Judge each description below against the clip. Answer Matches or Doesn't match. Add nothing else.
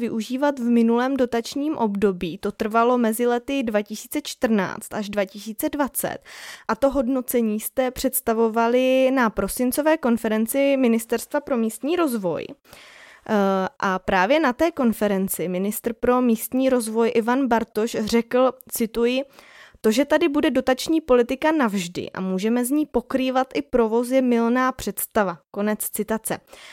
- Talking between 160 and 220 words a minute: Doesn't match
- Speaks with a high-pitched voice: Matches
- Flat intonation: Doesn't match